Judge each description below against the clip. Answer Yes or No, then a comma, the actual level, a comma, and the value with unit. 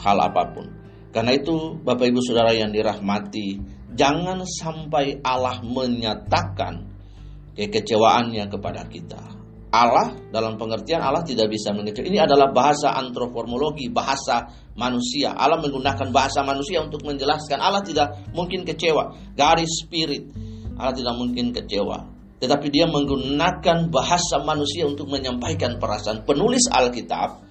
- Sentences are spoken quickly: No, average, 120 wpm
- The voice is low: Yes, low, 130 Hz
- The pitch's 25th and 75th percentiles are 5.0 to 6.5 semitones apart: Yes, wide, 5.5 semitones